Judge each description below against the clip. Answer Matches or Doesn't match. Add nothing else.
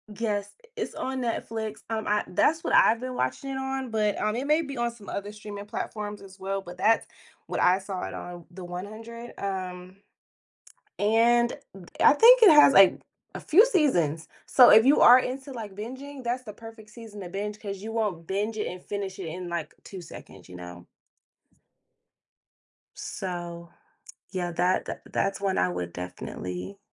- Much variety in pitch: Doesn't match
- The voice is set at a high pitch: Matches